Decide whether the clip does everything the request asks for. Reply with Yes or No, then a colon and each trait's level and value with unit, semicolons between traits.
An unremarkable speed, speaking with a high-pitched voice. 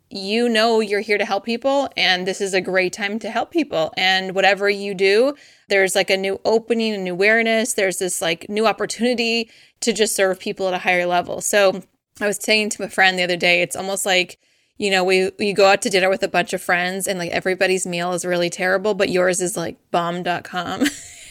No: fast, 225 wpm; high, 195 Hz